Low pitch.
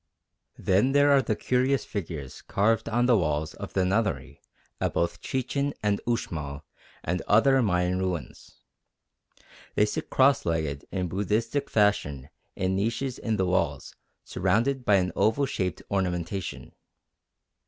Yes: low, 100 Hz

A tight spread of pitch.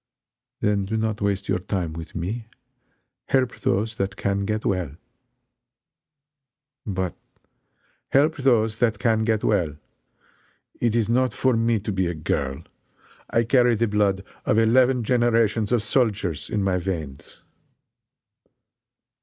No: average, 3.4 semitones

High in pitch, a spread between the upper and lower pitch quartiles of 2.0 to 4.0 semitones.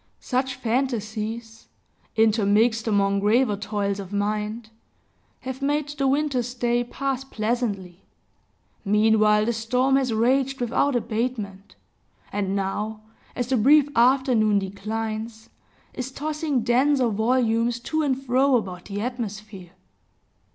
Yes: high, 230 Hz; average, 3.5 semitones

